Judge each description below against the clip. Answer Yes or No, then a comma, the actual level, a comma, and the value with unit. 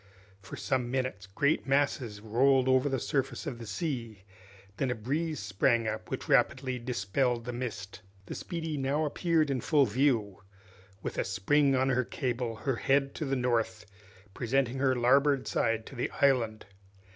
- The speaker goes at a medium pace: Yes, average, 165 wpm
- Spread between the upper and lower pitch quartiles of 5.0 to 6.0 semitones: No, average, 3.2 semitones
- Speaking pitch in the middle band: No, low, 130 Hz